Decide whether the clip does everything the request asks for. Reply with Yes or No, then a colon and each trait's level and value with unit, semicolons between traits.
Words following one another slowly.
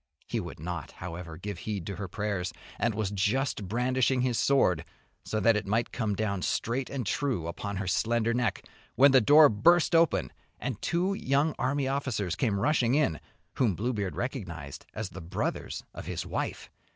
No: average, 175 wpm